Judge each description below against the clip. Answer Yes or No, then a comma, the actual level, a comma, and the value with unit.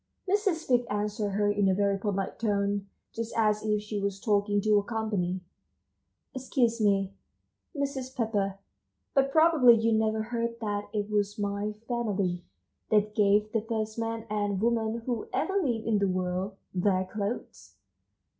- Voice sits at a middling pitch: No, high, 210 Hz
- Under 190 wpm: Yes, average, 150 wpm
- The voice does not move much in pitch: Yes, narrow, 2.3 semitones